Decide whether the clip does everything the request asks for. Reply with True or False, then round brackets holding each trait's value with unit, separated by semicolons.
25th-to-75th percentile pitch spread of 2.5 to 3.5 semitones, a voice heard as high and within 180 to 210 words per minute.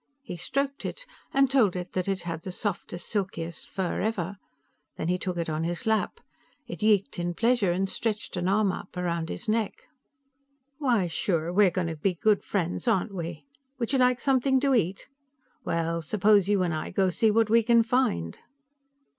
False (4.6 semitones; 195 Hz; 190 wpm)